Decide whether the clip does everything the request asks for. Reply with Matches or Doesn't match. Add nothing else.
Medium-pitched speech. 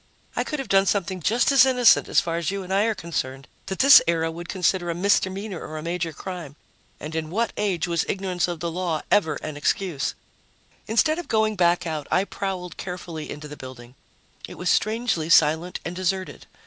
Matches